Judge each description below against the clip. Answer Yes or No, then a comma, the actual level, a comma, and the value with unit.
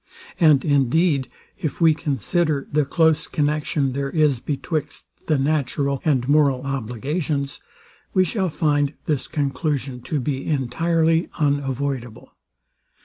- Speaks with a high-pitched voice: No, medium, 145 Hz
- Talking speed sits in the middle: No, slow, 115 wpm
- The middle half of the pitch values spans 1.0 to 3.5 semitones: Yes, narrow, 2.4 semitones